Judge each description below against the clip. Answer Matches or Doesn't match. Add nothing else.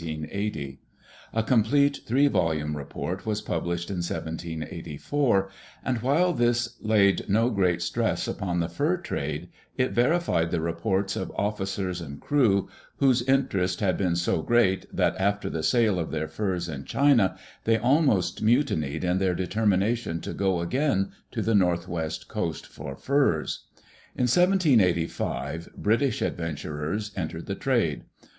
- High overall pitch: Doesn't match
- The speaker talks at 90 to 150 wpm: Matches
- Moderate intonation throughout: Doesn't match